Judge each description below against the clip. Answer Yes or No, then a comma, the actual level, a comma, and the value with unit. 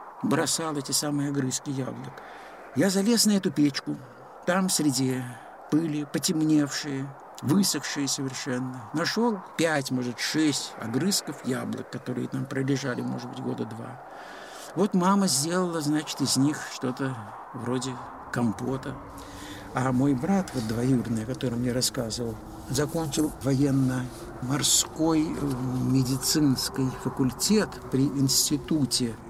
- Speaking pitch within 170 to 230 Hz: No, low, 135 Hz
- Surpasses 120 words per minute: No, slow, 110 wpm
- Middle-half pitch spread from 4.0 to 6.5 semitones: No, average, 3.2 semitones